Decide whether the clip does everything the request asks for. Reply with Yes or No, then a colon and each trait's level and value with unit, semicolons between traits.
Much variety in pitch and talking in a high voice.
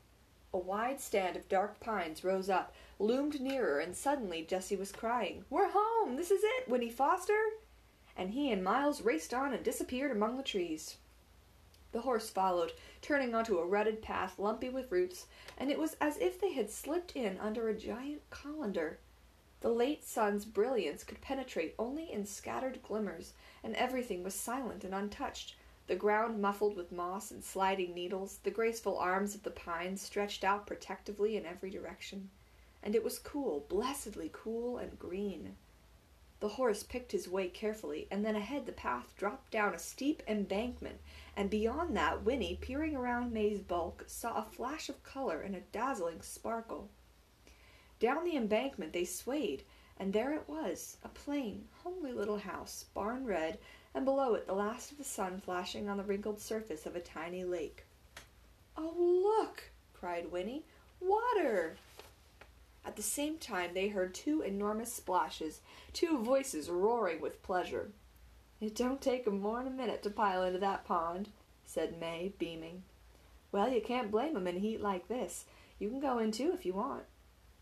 Yes: wide, 6.0 semitones; high, 215 Hz